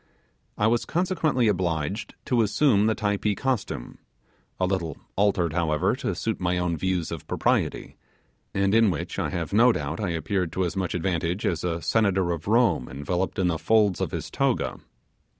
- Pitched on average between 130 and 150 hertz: No, very low, 95 Hz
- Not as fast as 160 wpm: No, average, 175 wpm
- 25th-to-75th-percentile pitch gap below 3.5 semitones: No, average, 4.0 semitones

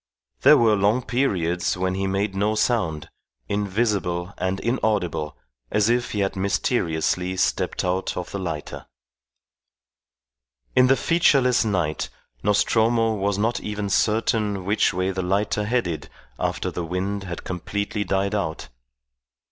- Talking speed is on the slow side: Yes, slow, 130 wpm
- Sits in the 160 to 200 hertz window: No, low, 100 Hz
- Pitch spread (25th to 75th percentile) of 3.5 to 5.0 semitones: No, average, 2.9 semitones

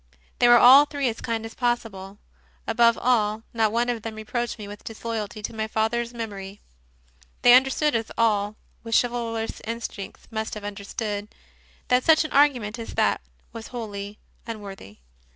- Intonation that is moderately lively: No, narrow, 2.3 semitones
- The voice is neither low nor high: No, high, 225 Hz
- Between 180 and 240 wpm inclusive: No, average, 170 wpm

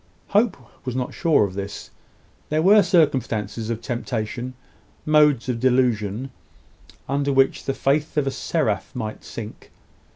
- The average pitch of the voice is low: Yes, low, 130 Hz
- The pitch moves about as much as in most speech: Yes, average, 4.8 semitones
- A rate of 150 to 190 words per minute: No, slow, 135 wpm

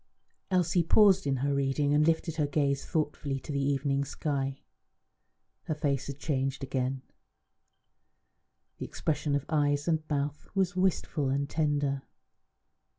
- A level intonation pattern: Yes, narrow, 2.1 semitones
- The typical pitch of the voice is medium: Yes, medium, 145 Hz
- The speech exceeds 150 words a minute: No, slow, 135 wpm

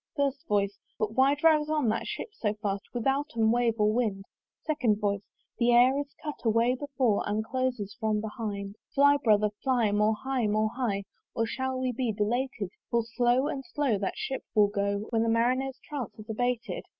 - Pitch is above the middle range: Yes, high, 230 Hz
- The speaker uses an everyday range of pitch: Yes, average, 3.8 semitones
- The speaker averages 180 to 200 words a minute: Yes, average, 185 wpm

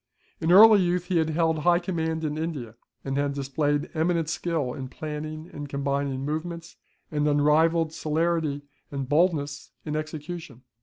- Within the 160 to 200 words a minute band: No, average, 150 wpm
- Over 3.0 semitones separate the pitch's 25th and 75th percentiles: No, narrow, 2.6 semitones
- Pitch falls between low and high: Yes, medium, 155 Hz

